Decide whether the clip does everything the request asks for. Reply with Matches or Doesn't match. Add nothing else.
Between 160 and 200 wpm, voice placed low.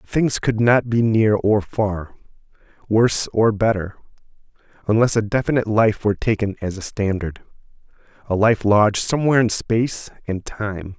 Doesn't match